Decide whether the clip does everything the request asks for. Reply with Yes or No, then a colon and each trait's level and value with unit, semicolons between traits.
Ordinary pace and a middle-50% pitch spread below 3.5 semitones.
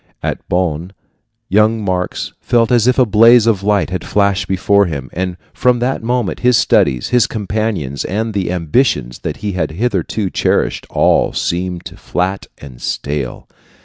No: average, 155 wpm; average, 4.2 semitones